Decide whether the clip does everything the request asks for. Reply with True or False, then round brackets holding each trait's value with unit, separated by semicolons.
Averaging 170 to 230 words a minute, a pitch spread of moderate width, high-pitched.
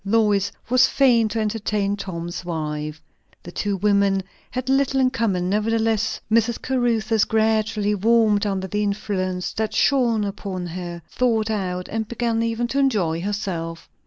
False (145 wpm; 3.2 semitones; 210 Hz)